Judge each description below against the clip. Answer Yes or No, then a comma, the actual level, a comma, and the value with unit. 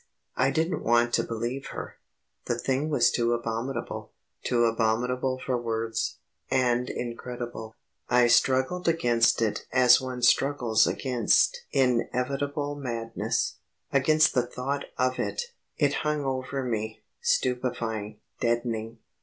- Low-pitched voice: Yes, low, 125 Hz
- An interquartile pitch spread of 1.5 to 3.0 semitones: Yes, narrow, 2.6 semitones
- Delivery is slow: Yes, slow, 120 wpm